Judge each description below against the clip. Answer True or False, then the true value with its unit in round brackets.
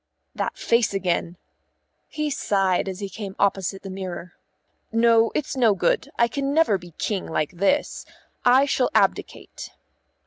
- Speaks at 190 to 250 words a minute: False (145 wpm)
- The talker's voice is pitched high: True (200 Hz)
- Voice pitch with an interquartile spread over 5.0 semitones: False (4.4 semitones)